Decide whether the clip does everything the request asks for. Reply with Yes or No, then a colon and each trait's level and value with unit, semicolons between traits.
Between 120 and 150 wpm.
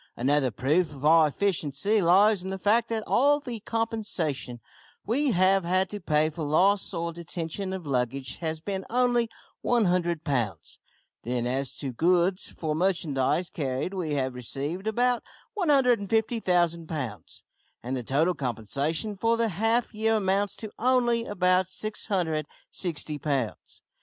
Yes: average, 140 wpm